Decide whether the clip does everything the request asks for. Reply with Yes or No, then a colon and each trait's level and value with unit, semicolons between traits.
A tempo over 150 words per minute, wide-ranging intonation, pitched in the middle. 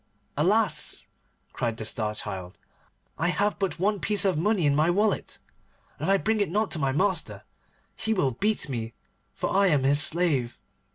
Yes: average, 180 wpm; wide, 7.1 semitones; medium, 175 Hz